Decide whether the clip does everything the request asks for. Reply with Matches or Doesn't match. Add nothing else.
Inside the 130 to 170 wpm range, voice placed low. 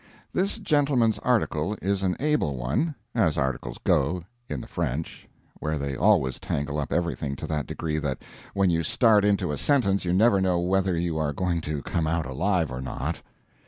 Doesn't match